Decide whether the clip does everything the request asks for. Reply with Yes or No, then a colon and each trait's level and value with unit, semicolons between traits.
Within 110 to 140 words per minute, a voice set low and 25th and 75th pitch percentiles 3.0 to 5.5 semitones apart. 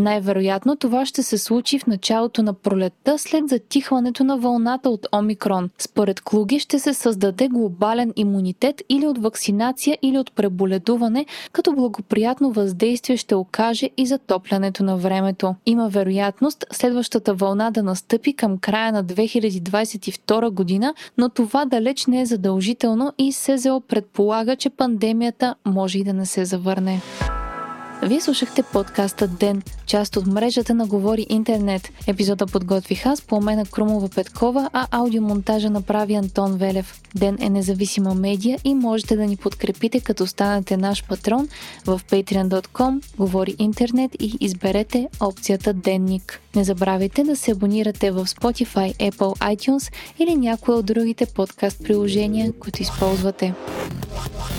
No: average, 135 wpm; high, 215 Hz; average, 4.0 semitones